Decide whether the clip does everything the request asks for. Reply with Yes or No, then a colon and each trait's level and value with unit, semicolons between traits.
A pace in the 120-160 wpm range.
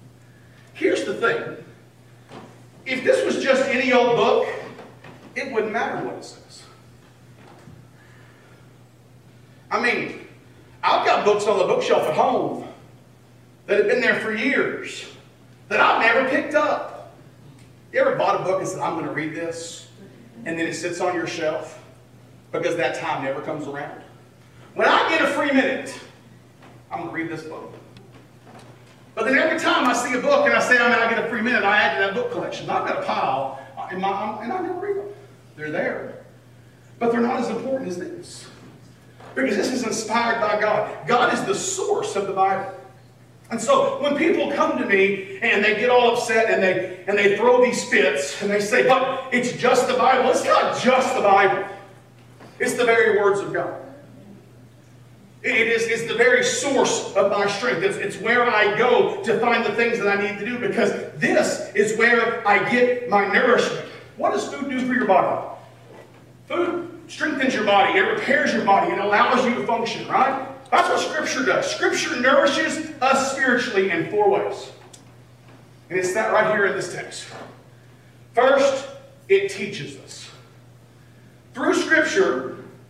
No: average, 180 wpm